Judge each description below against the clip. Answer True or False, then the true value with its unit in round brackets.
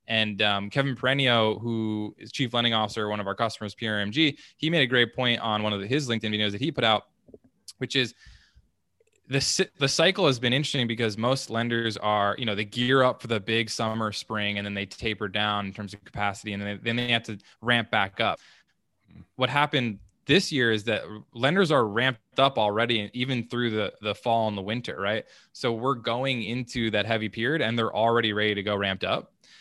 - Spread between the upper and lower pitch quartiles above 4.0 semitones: False (3.2 semitones)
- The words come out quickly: True (215 wpm)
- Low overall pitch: True (115 Hz)